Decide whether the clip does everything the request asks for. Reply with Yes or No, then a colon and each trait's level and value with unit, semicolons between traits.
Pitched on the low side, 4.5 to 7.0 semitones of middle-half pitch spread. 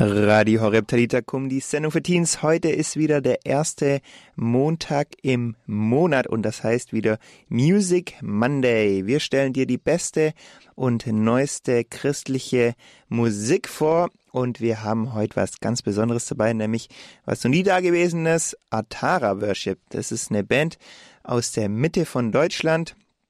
Yes: low, 125 Hz; average, 5.2 semitones